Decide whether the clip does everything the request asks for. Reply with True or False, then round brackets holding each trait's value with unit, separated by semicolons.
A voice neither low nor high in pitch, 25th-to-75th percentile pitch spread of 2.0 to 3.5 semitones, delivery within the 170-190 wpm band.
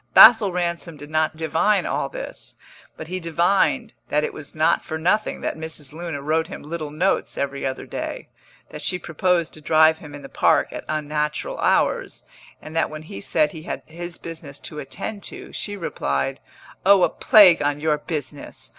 True (160 Hz; 2.6 semitones; 185 wpm)